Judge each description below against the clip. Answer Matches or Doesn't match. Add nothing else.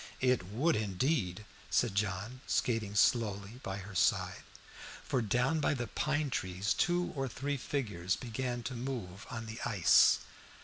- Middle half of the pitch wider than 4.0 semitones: Matches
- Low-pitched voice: Matches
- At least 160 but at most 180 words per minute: Doesn't match